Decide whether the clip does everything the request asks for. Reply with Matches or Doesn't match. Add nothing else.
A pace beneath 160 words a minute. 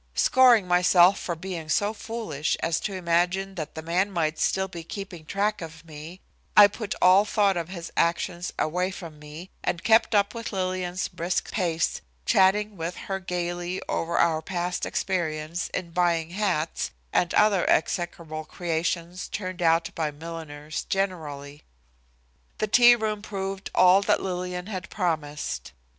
Matches